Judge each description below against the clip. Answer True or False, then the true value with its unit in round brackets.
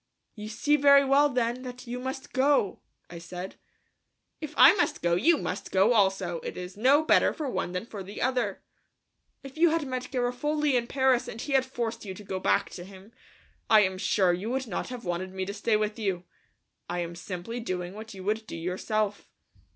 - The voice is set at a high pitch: True (220 Hz)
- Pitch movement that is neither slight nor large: False (5.7 semitones)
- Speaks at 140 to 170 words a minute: False (205 wpm)